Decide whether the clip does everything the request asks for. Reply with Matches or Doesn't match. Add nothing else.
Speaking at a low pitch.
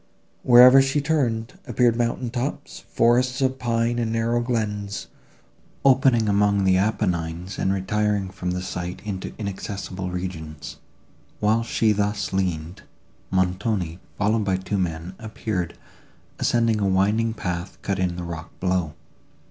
Matches